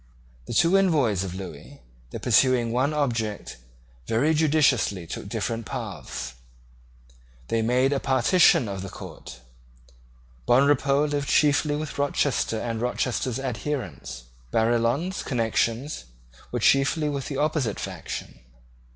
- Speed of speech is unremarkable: No, slow, 115 wpm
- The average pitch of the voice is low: Yes, low, 130 Hz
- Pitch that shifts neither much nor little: Yes, average, 4.5 semitones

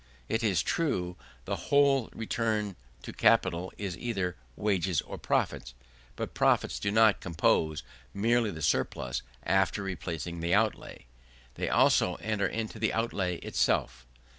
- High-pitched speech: No, low, 100 Hz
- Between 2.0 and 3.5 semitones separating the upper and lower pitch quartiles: No, average, 4.4 semitones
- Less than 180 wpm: Yes, slow, 135 wpm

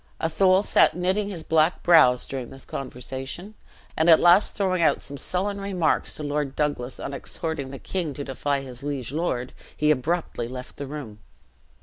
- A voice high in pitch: No, medium, 150 Hz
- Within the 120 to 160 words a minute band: No, average, 170 wpm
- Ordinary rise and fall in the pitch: Yes, average, 4.7 semitones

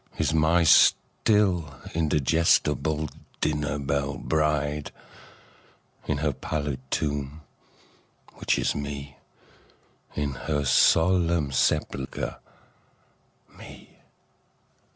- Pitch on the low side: Yes, very low, 75 Hz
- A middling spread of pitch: No, narrow, 2.0 semitones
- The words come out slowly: Yes, slow, 75 wpm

